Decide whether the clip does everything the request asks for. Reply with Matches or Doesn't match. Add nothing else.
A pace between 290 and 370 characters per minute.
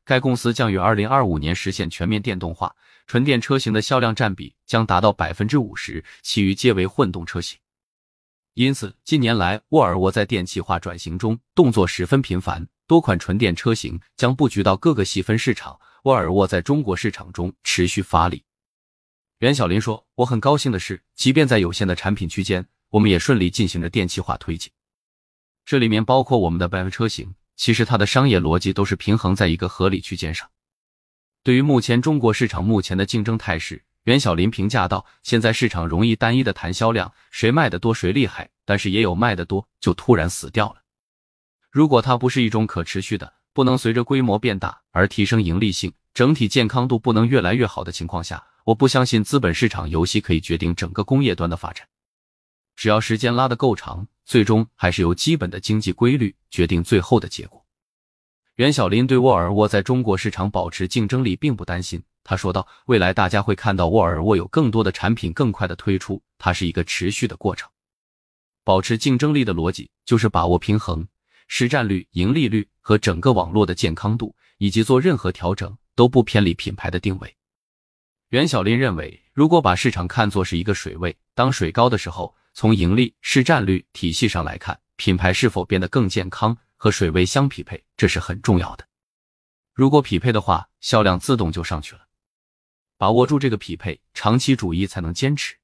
Matches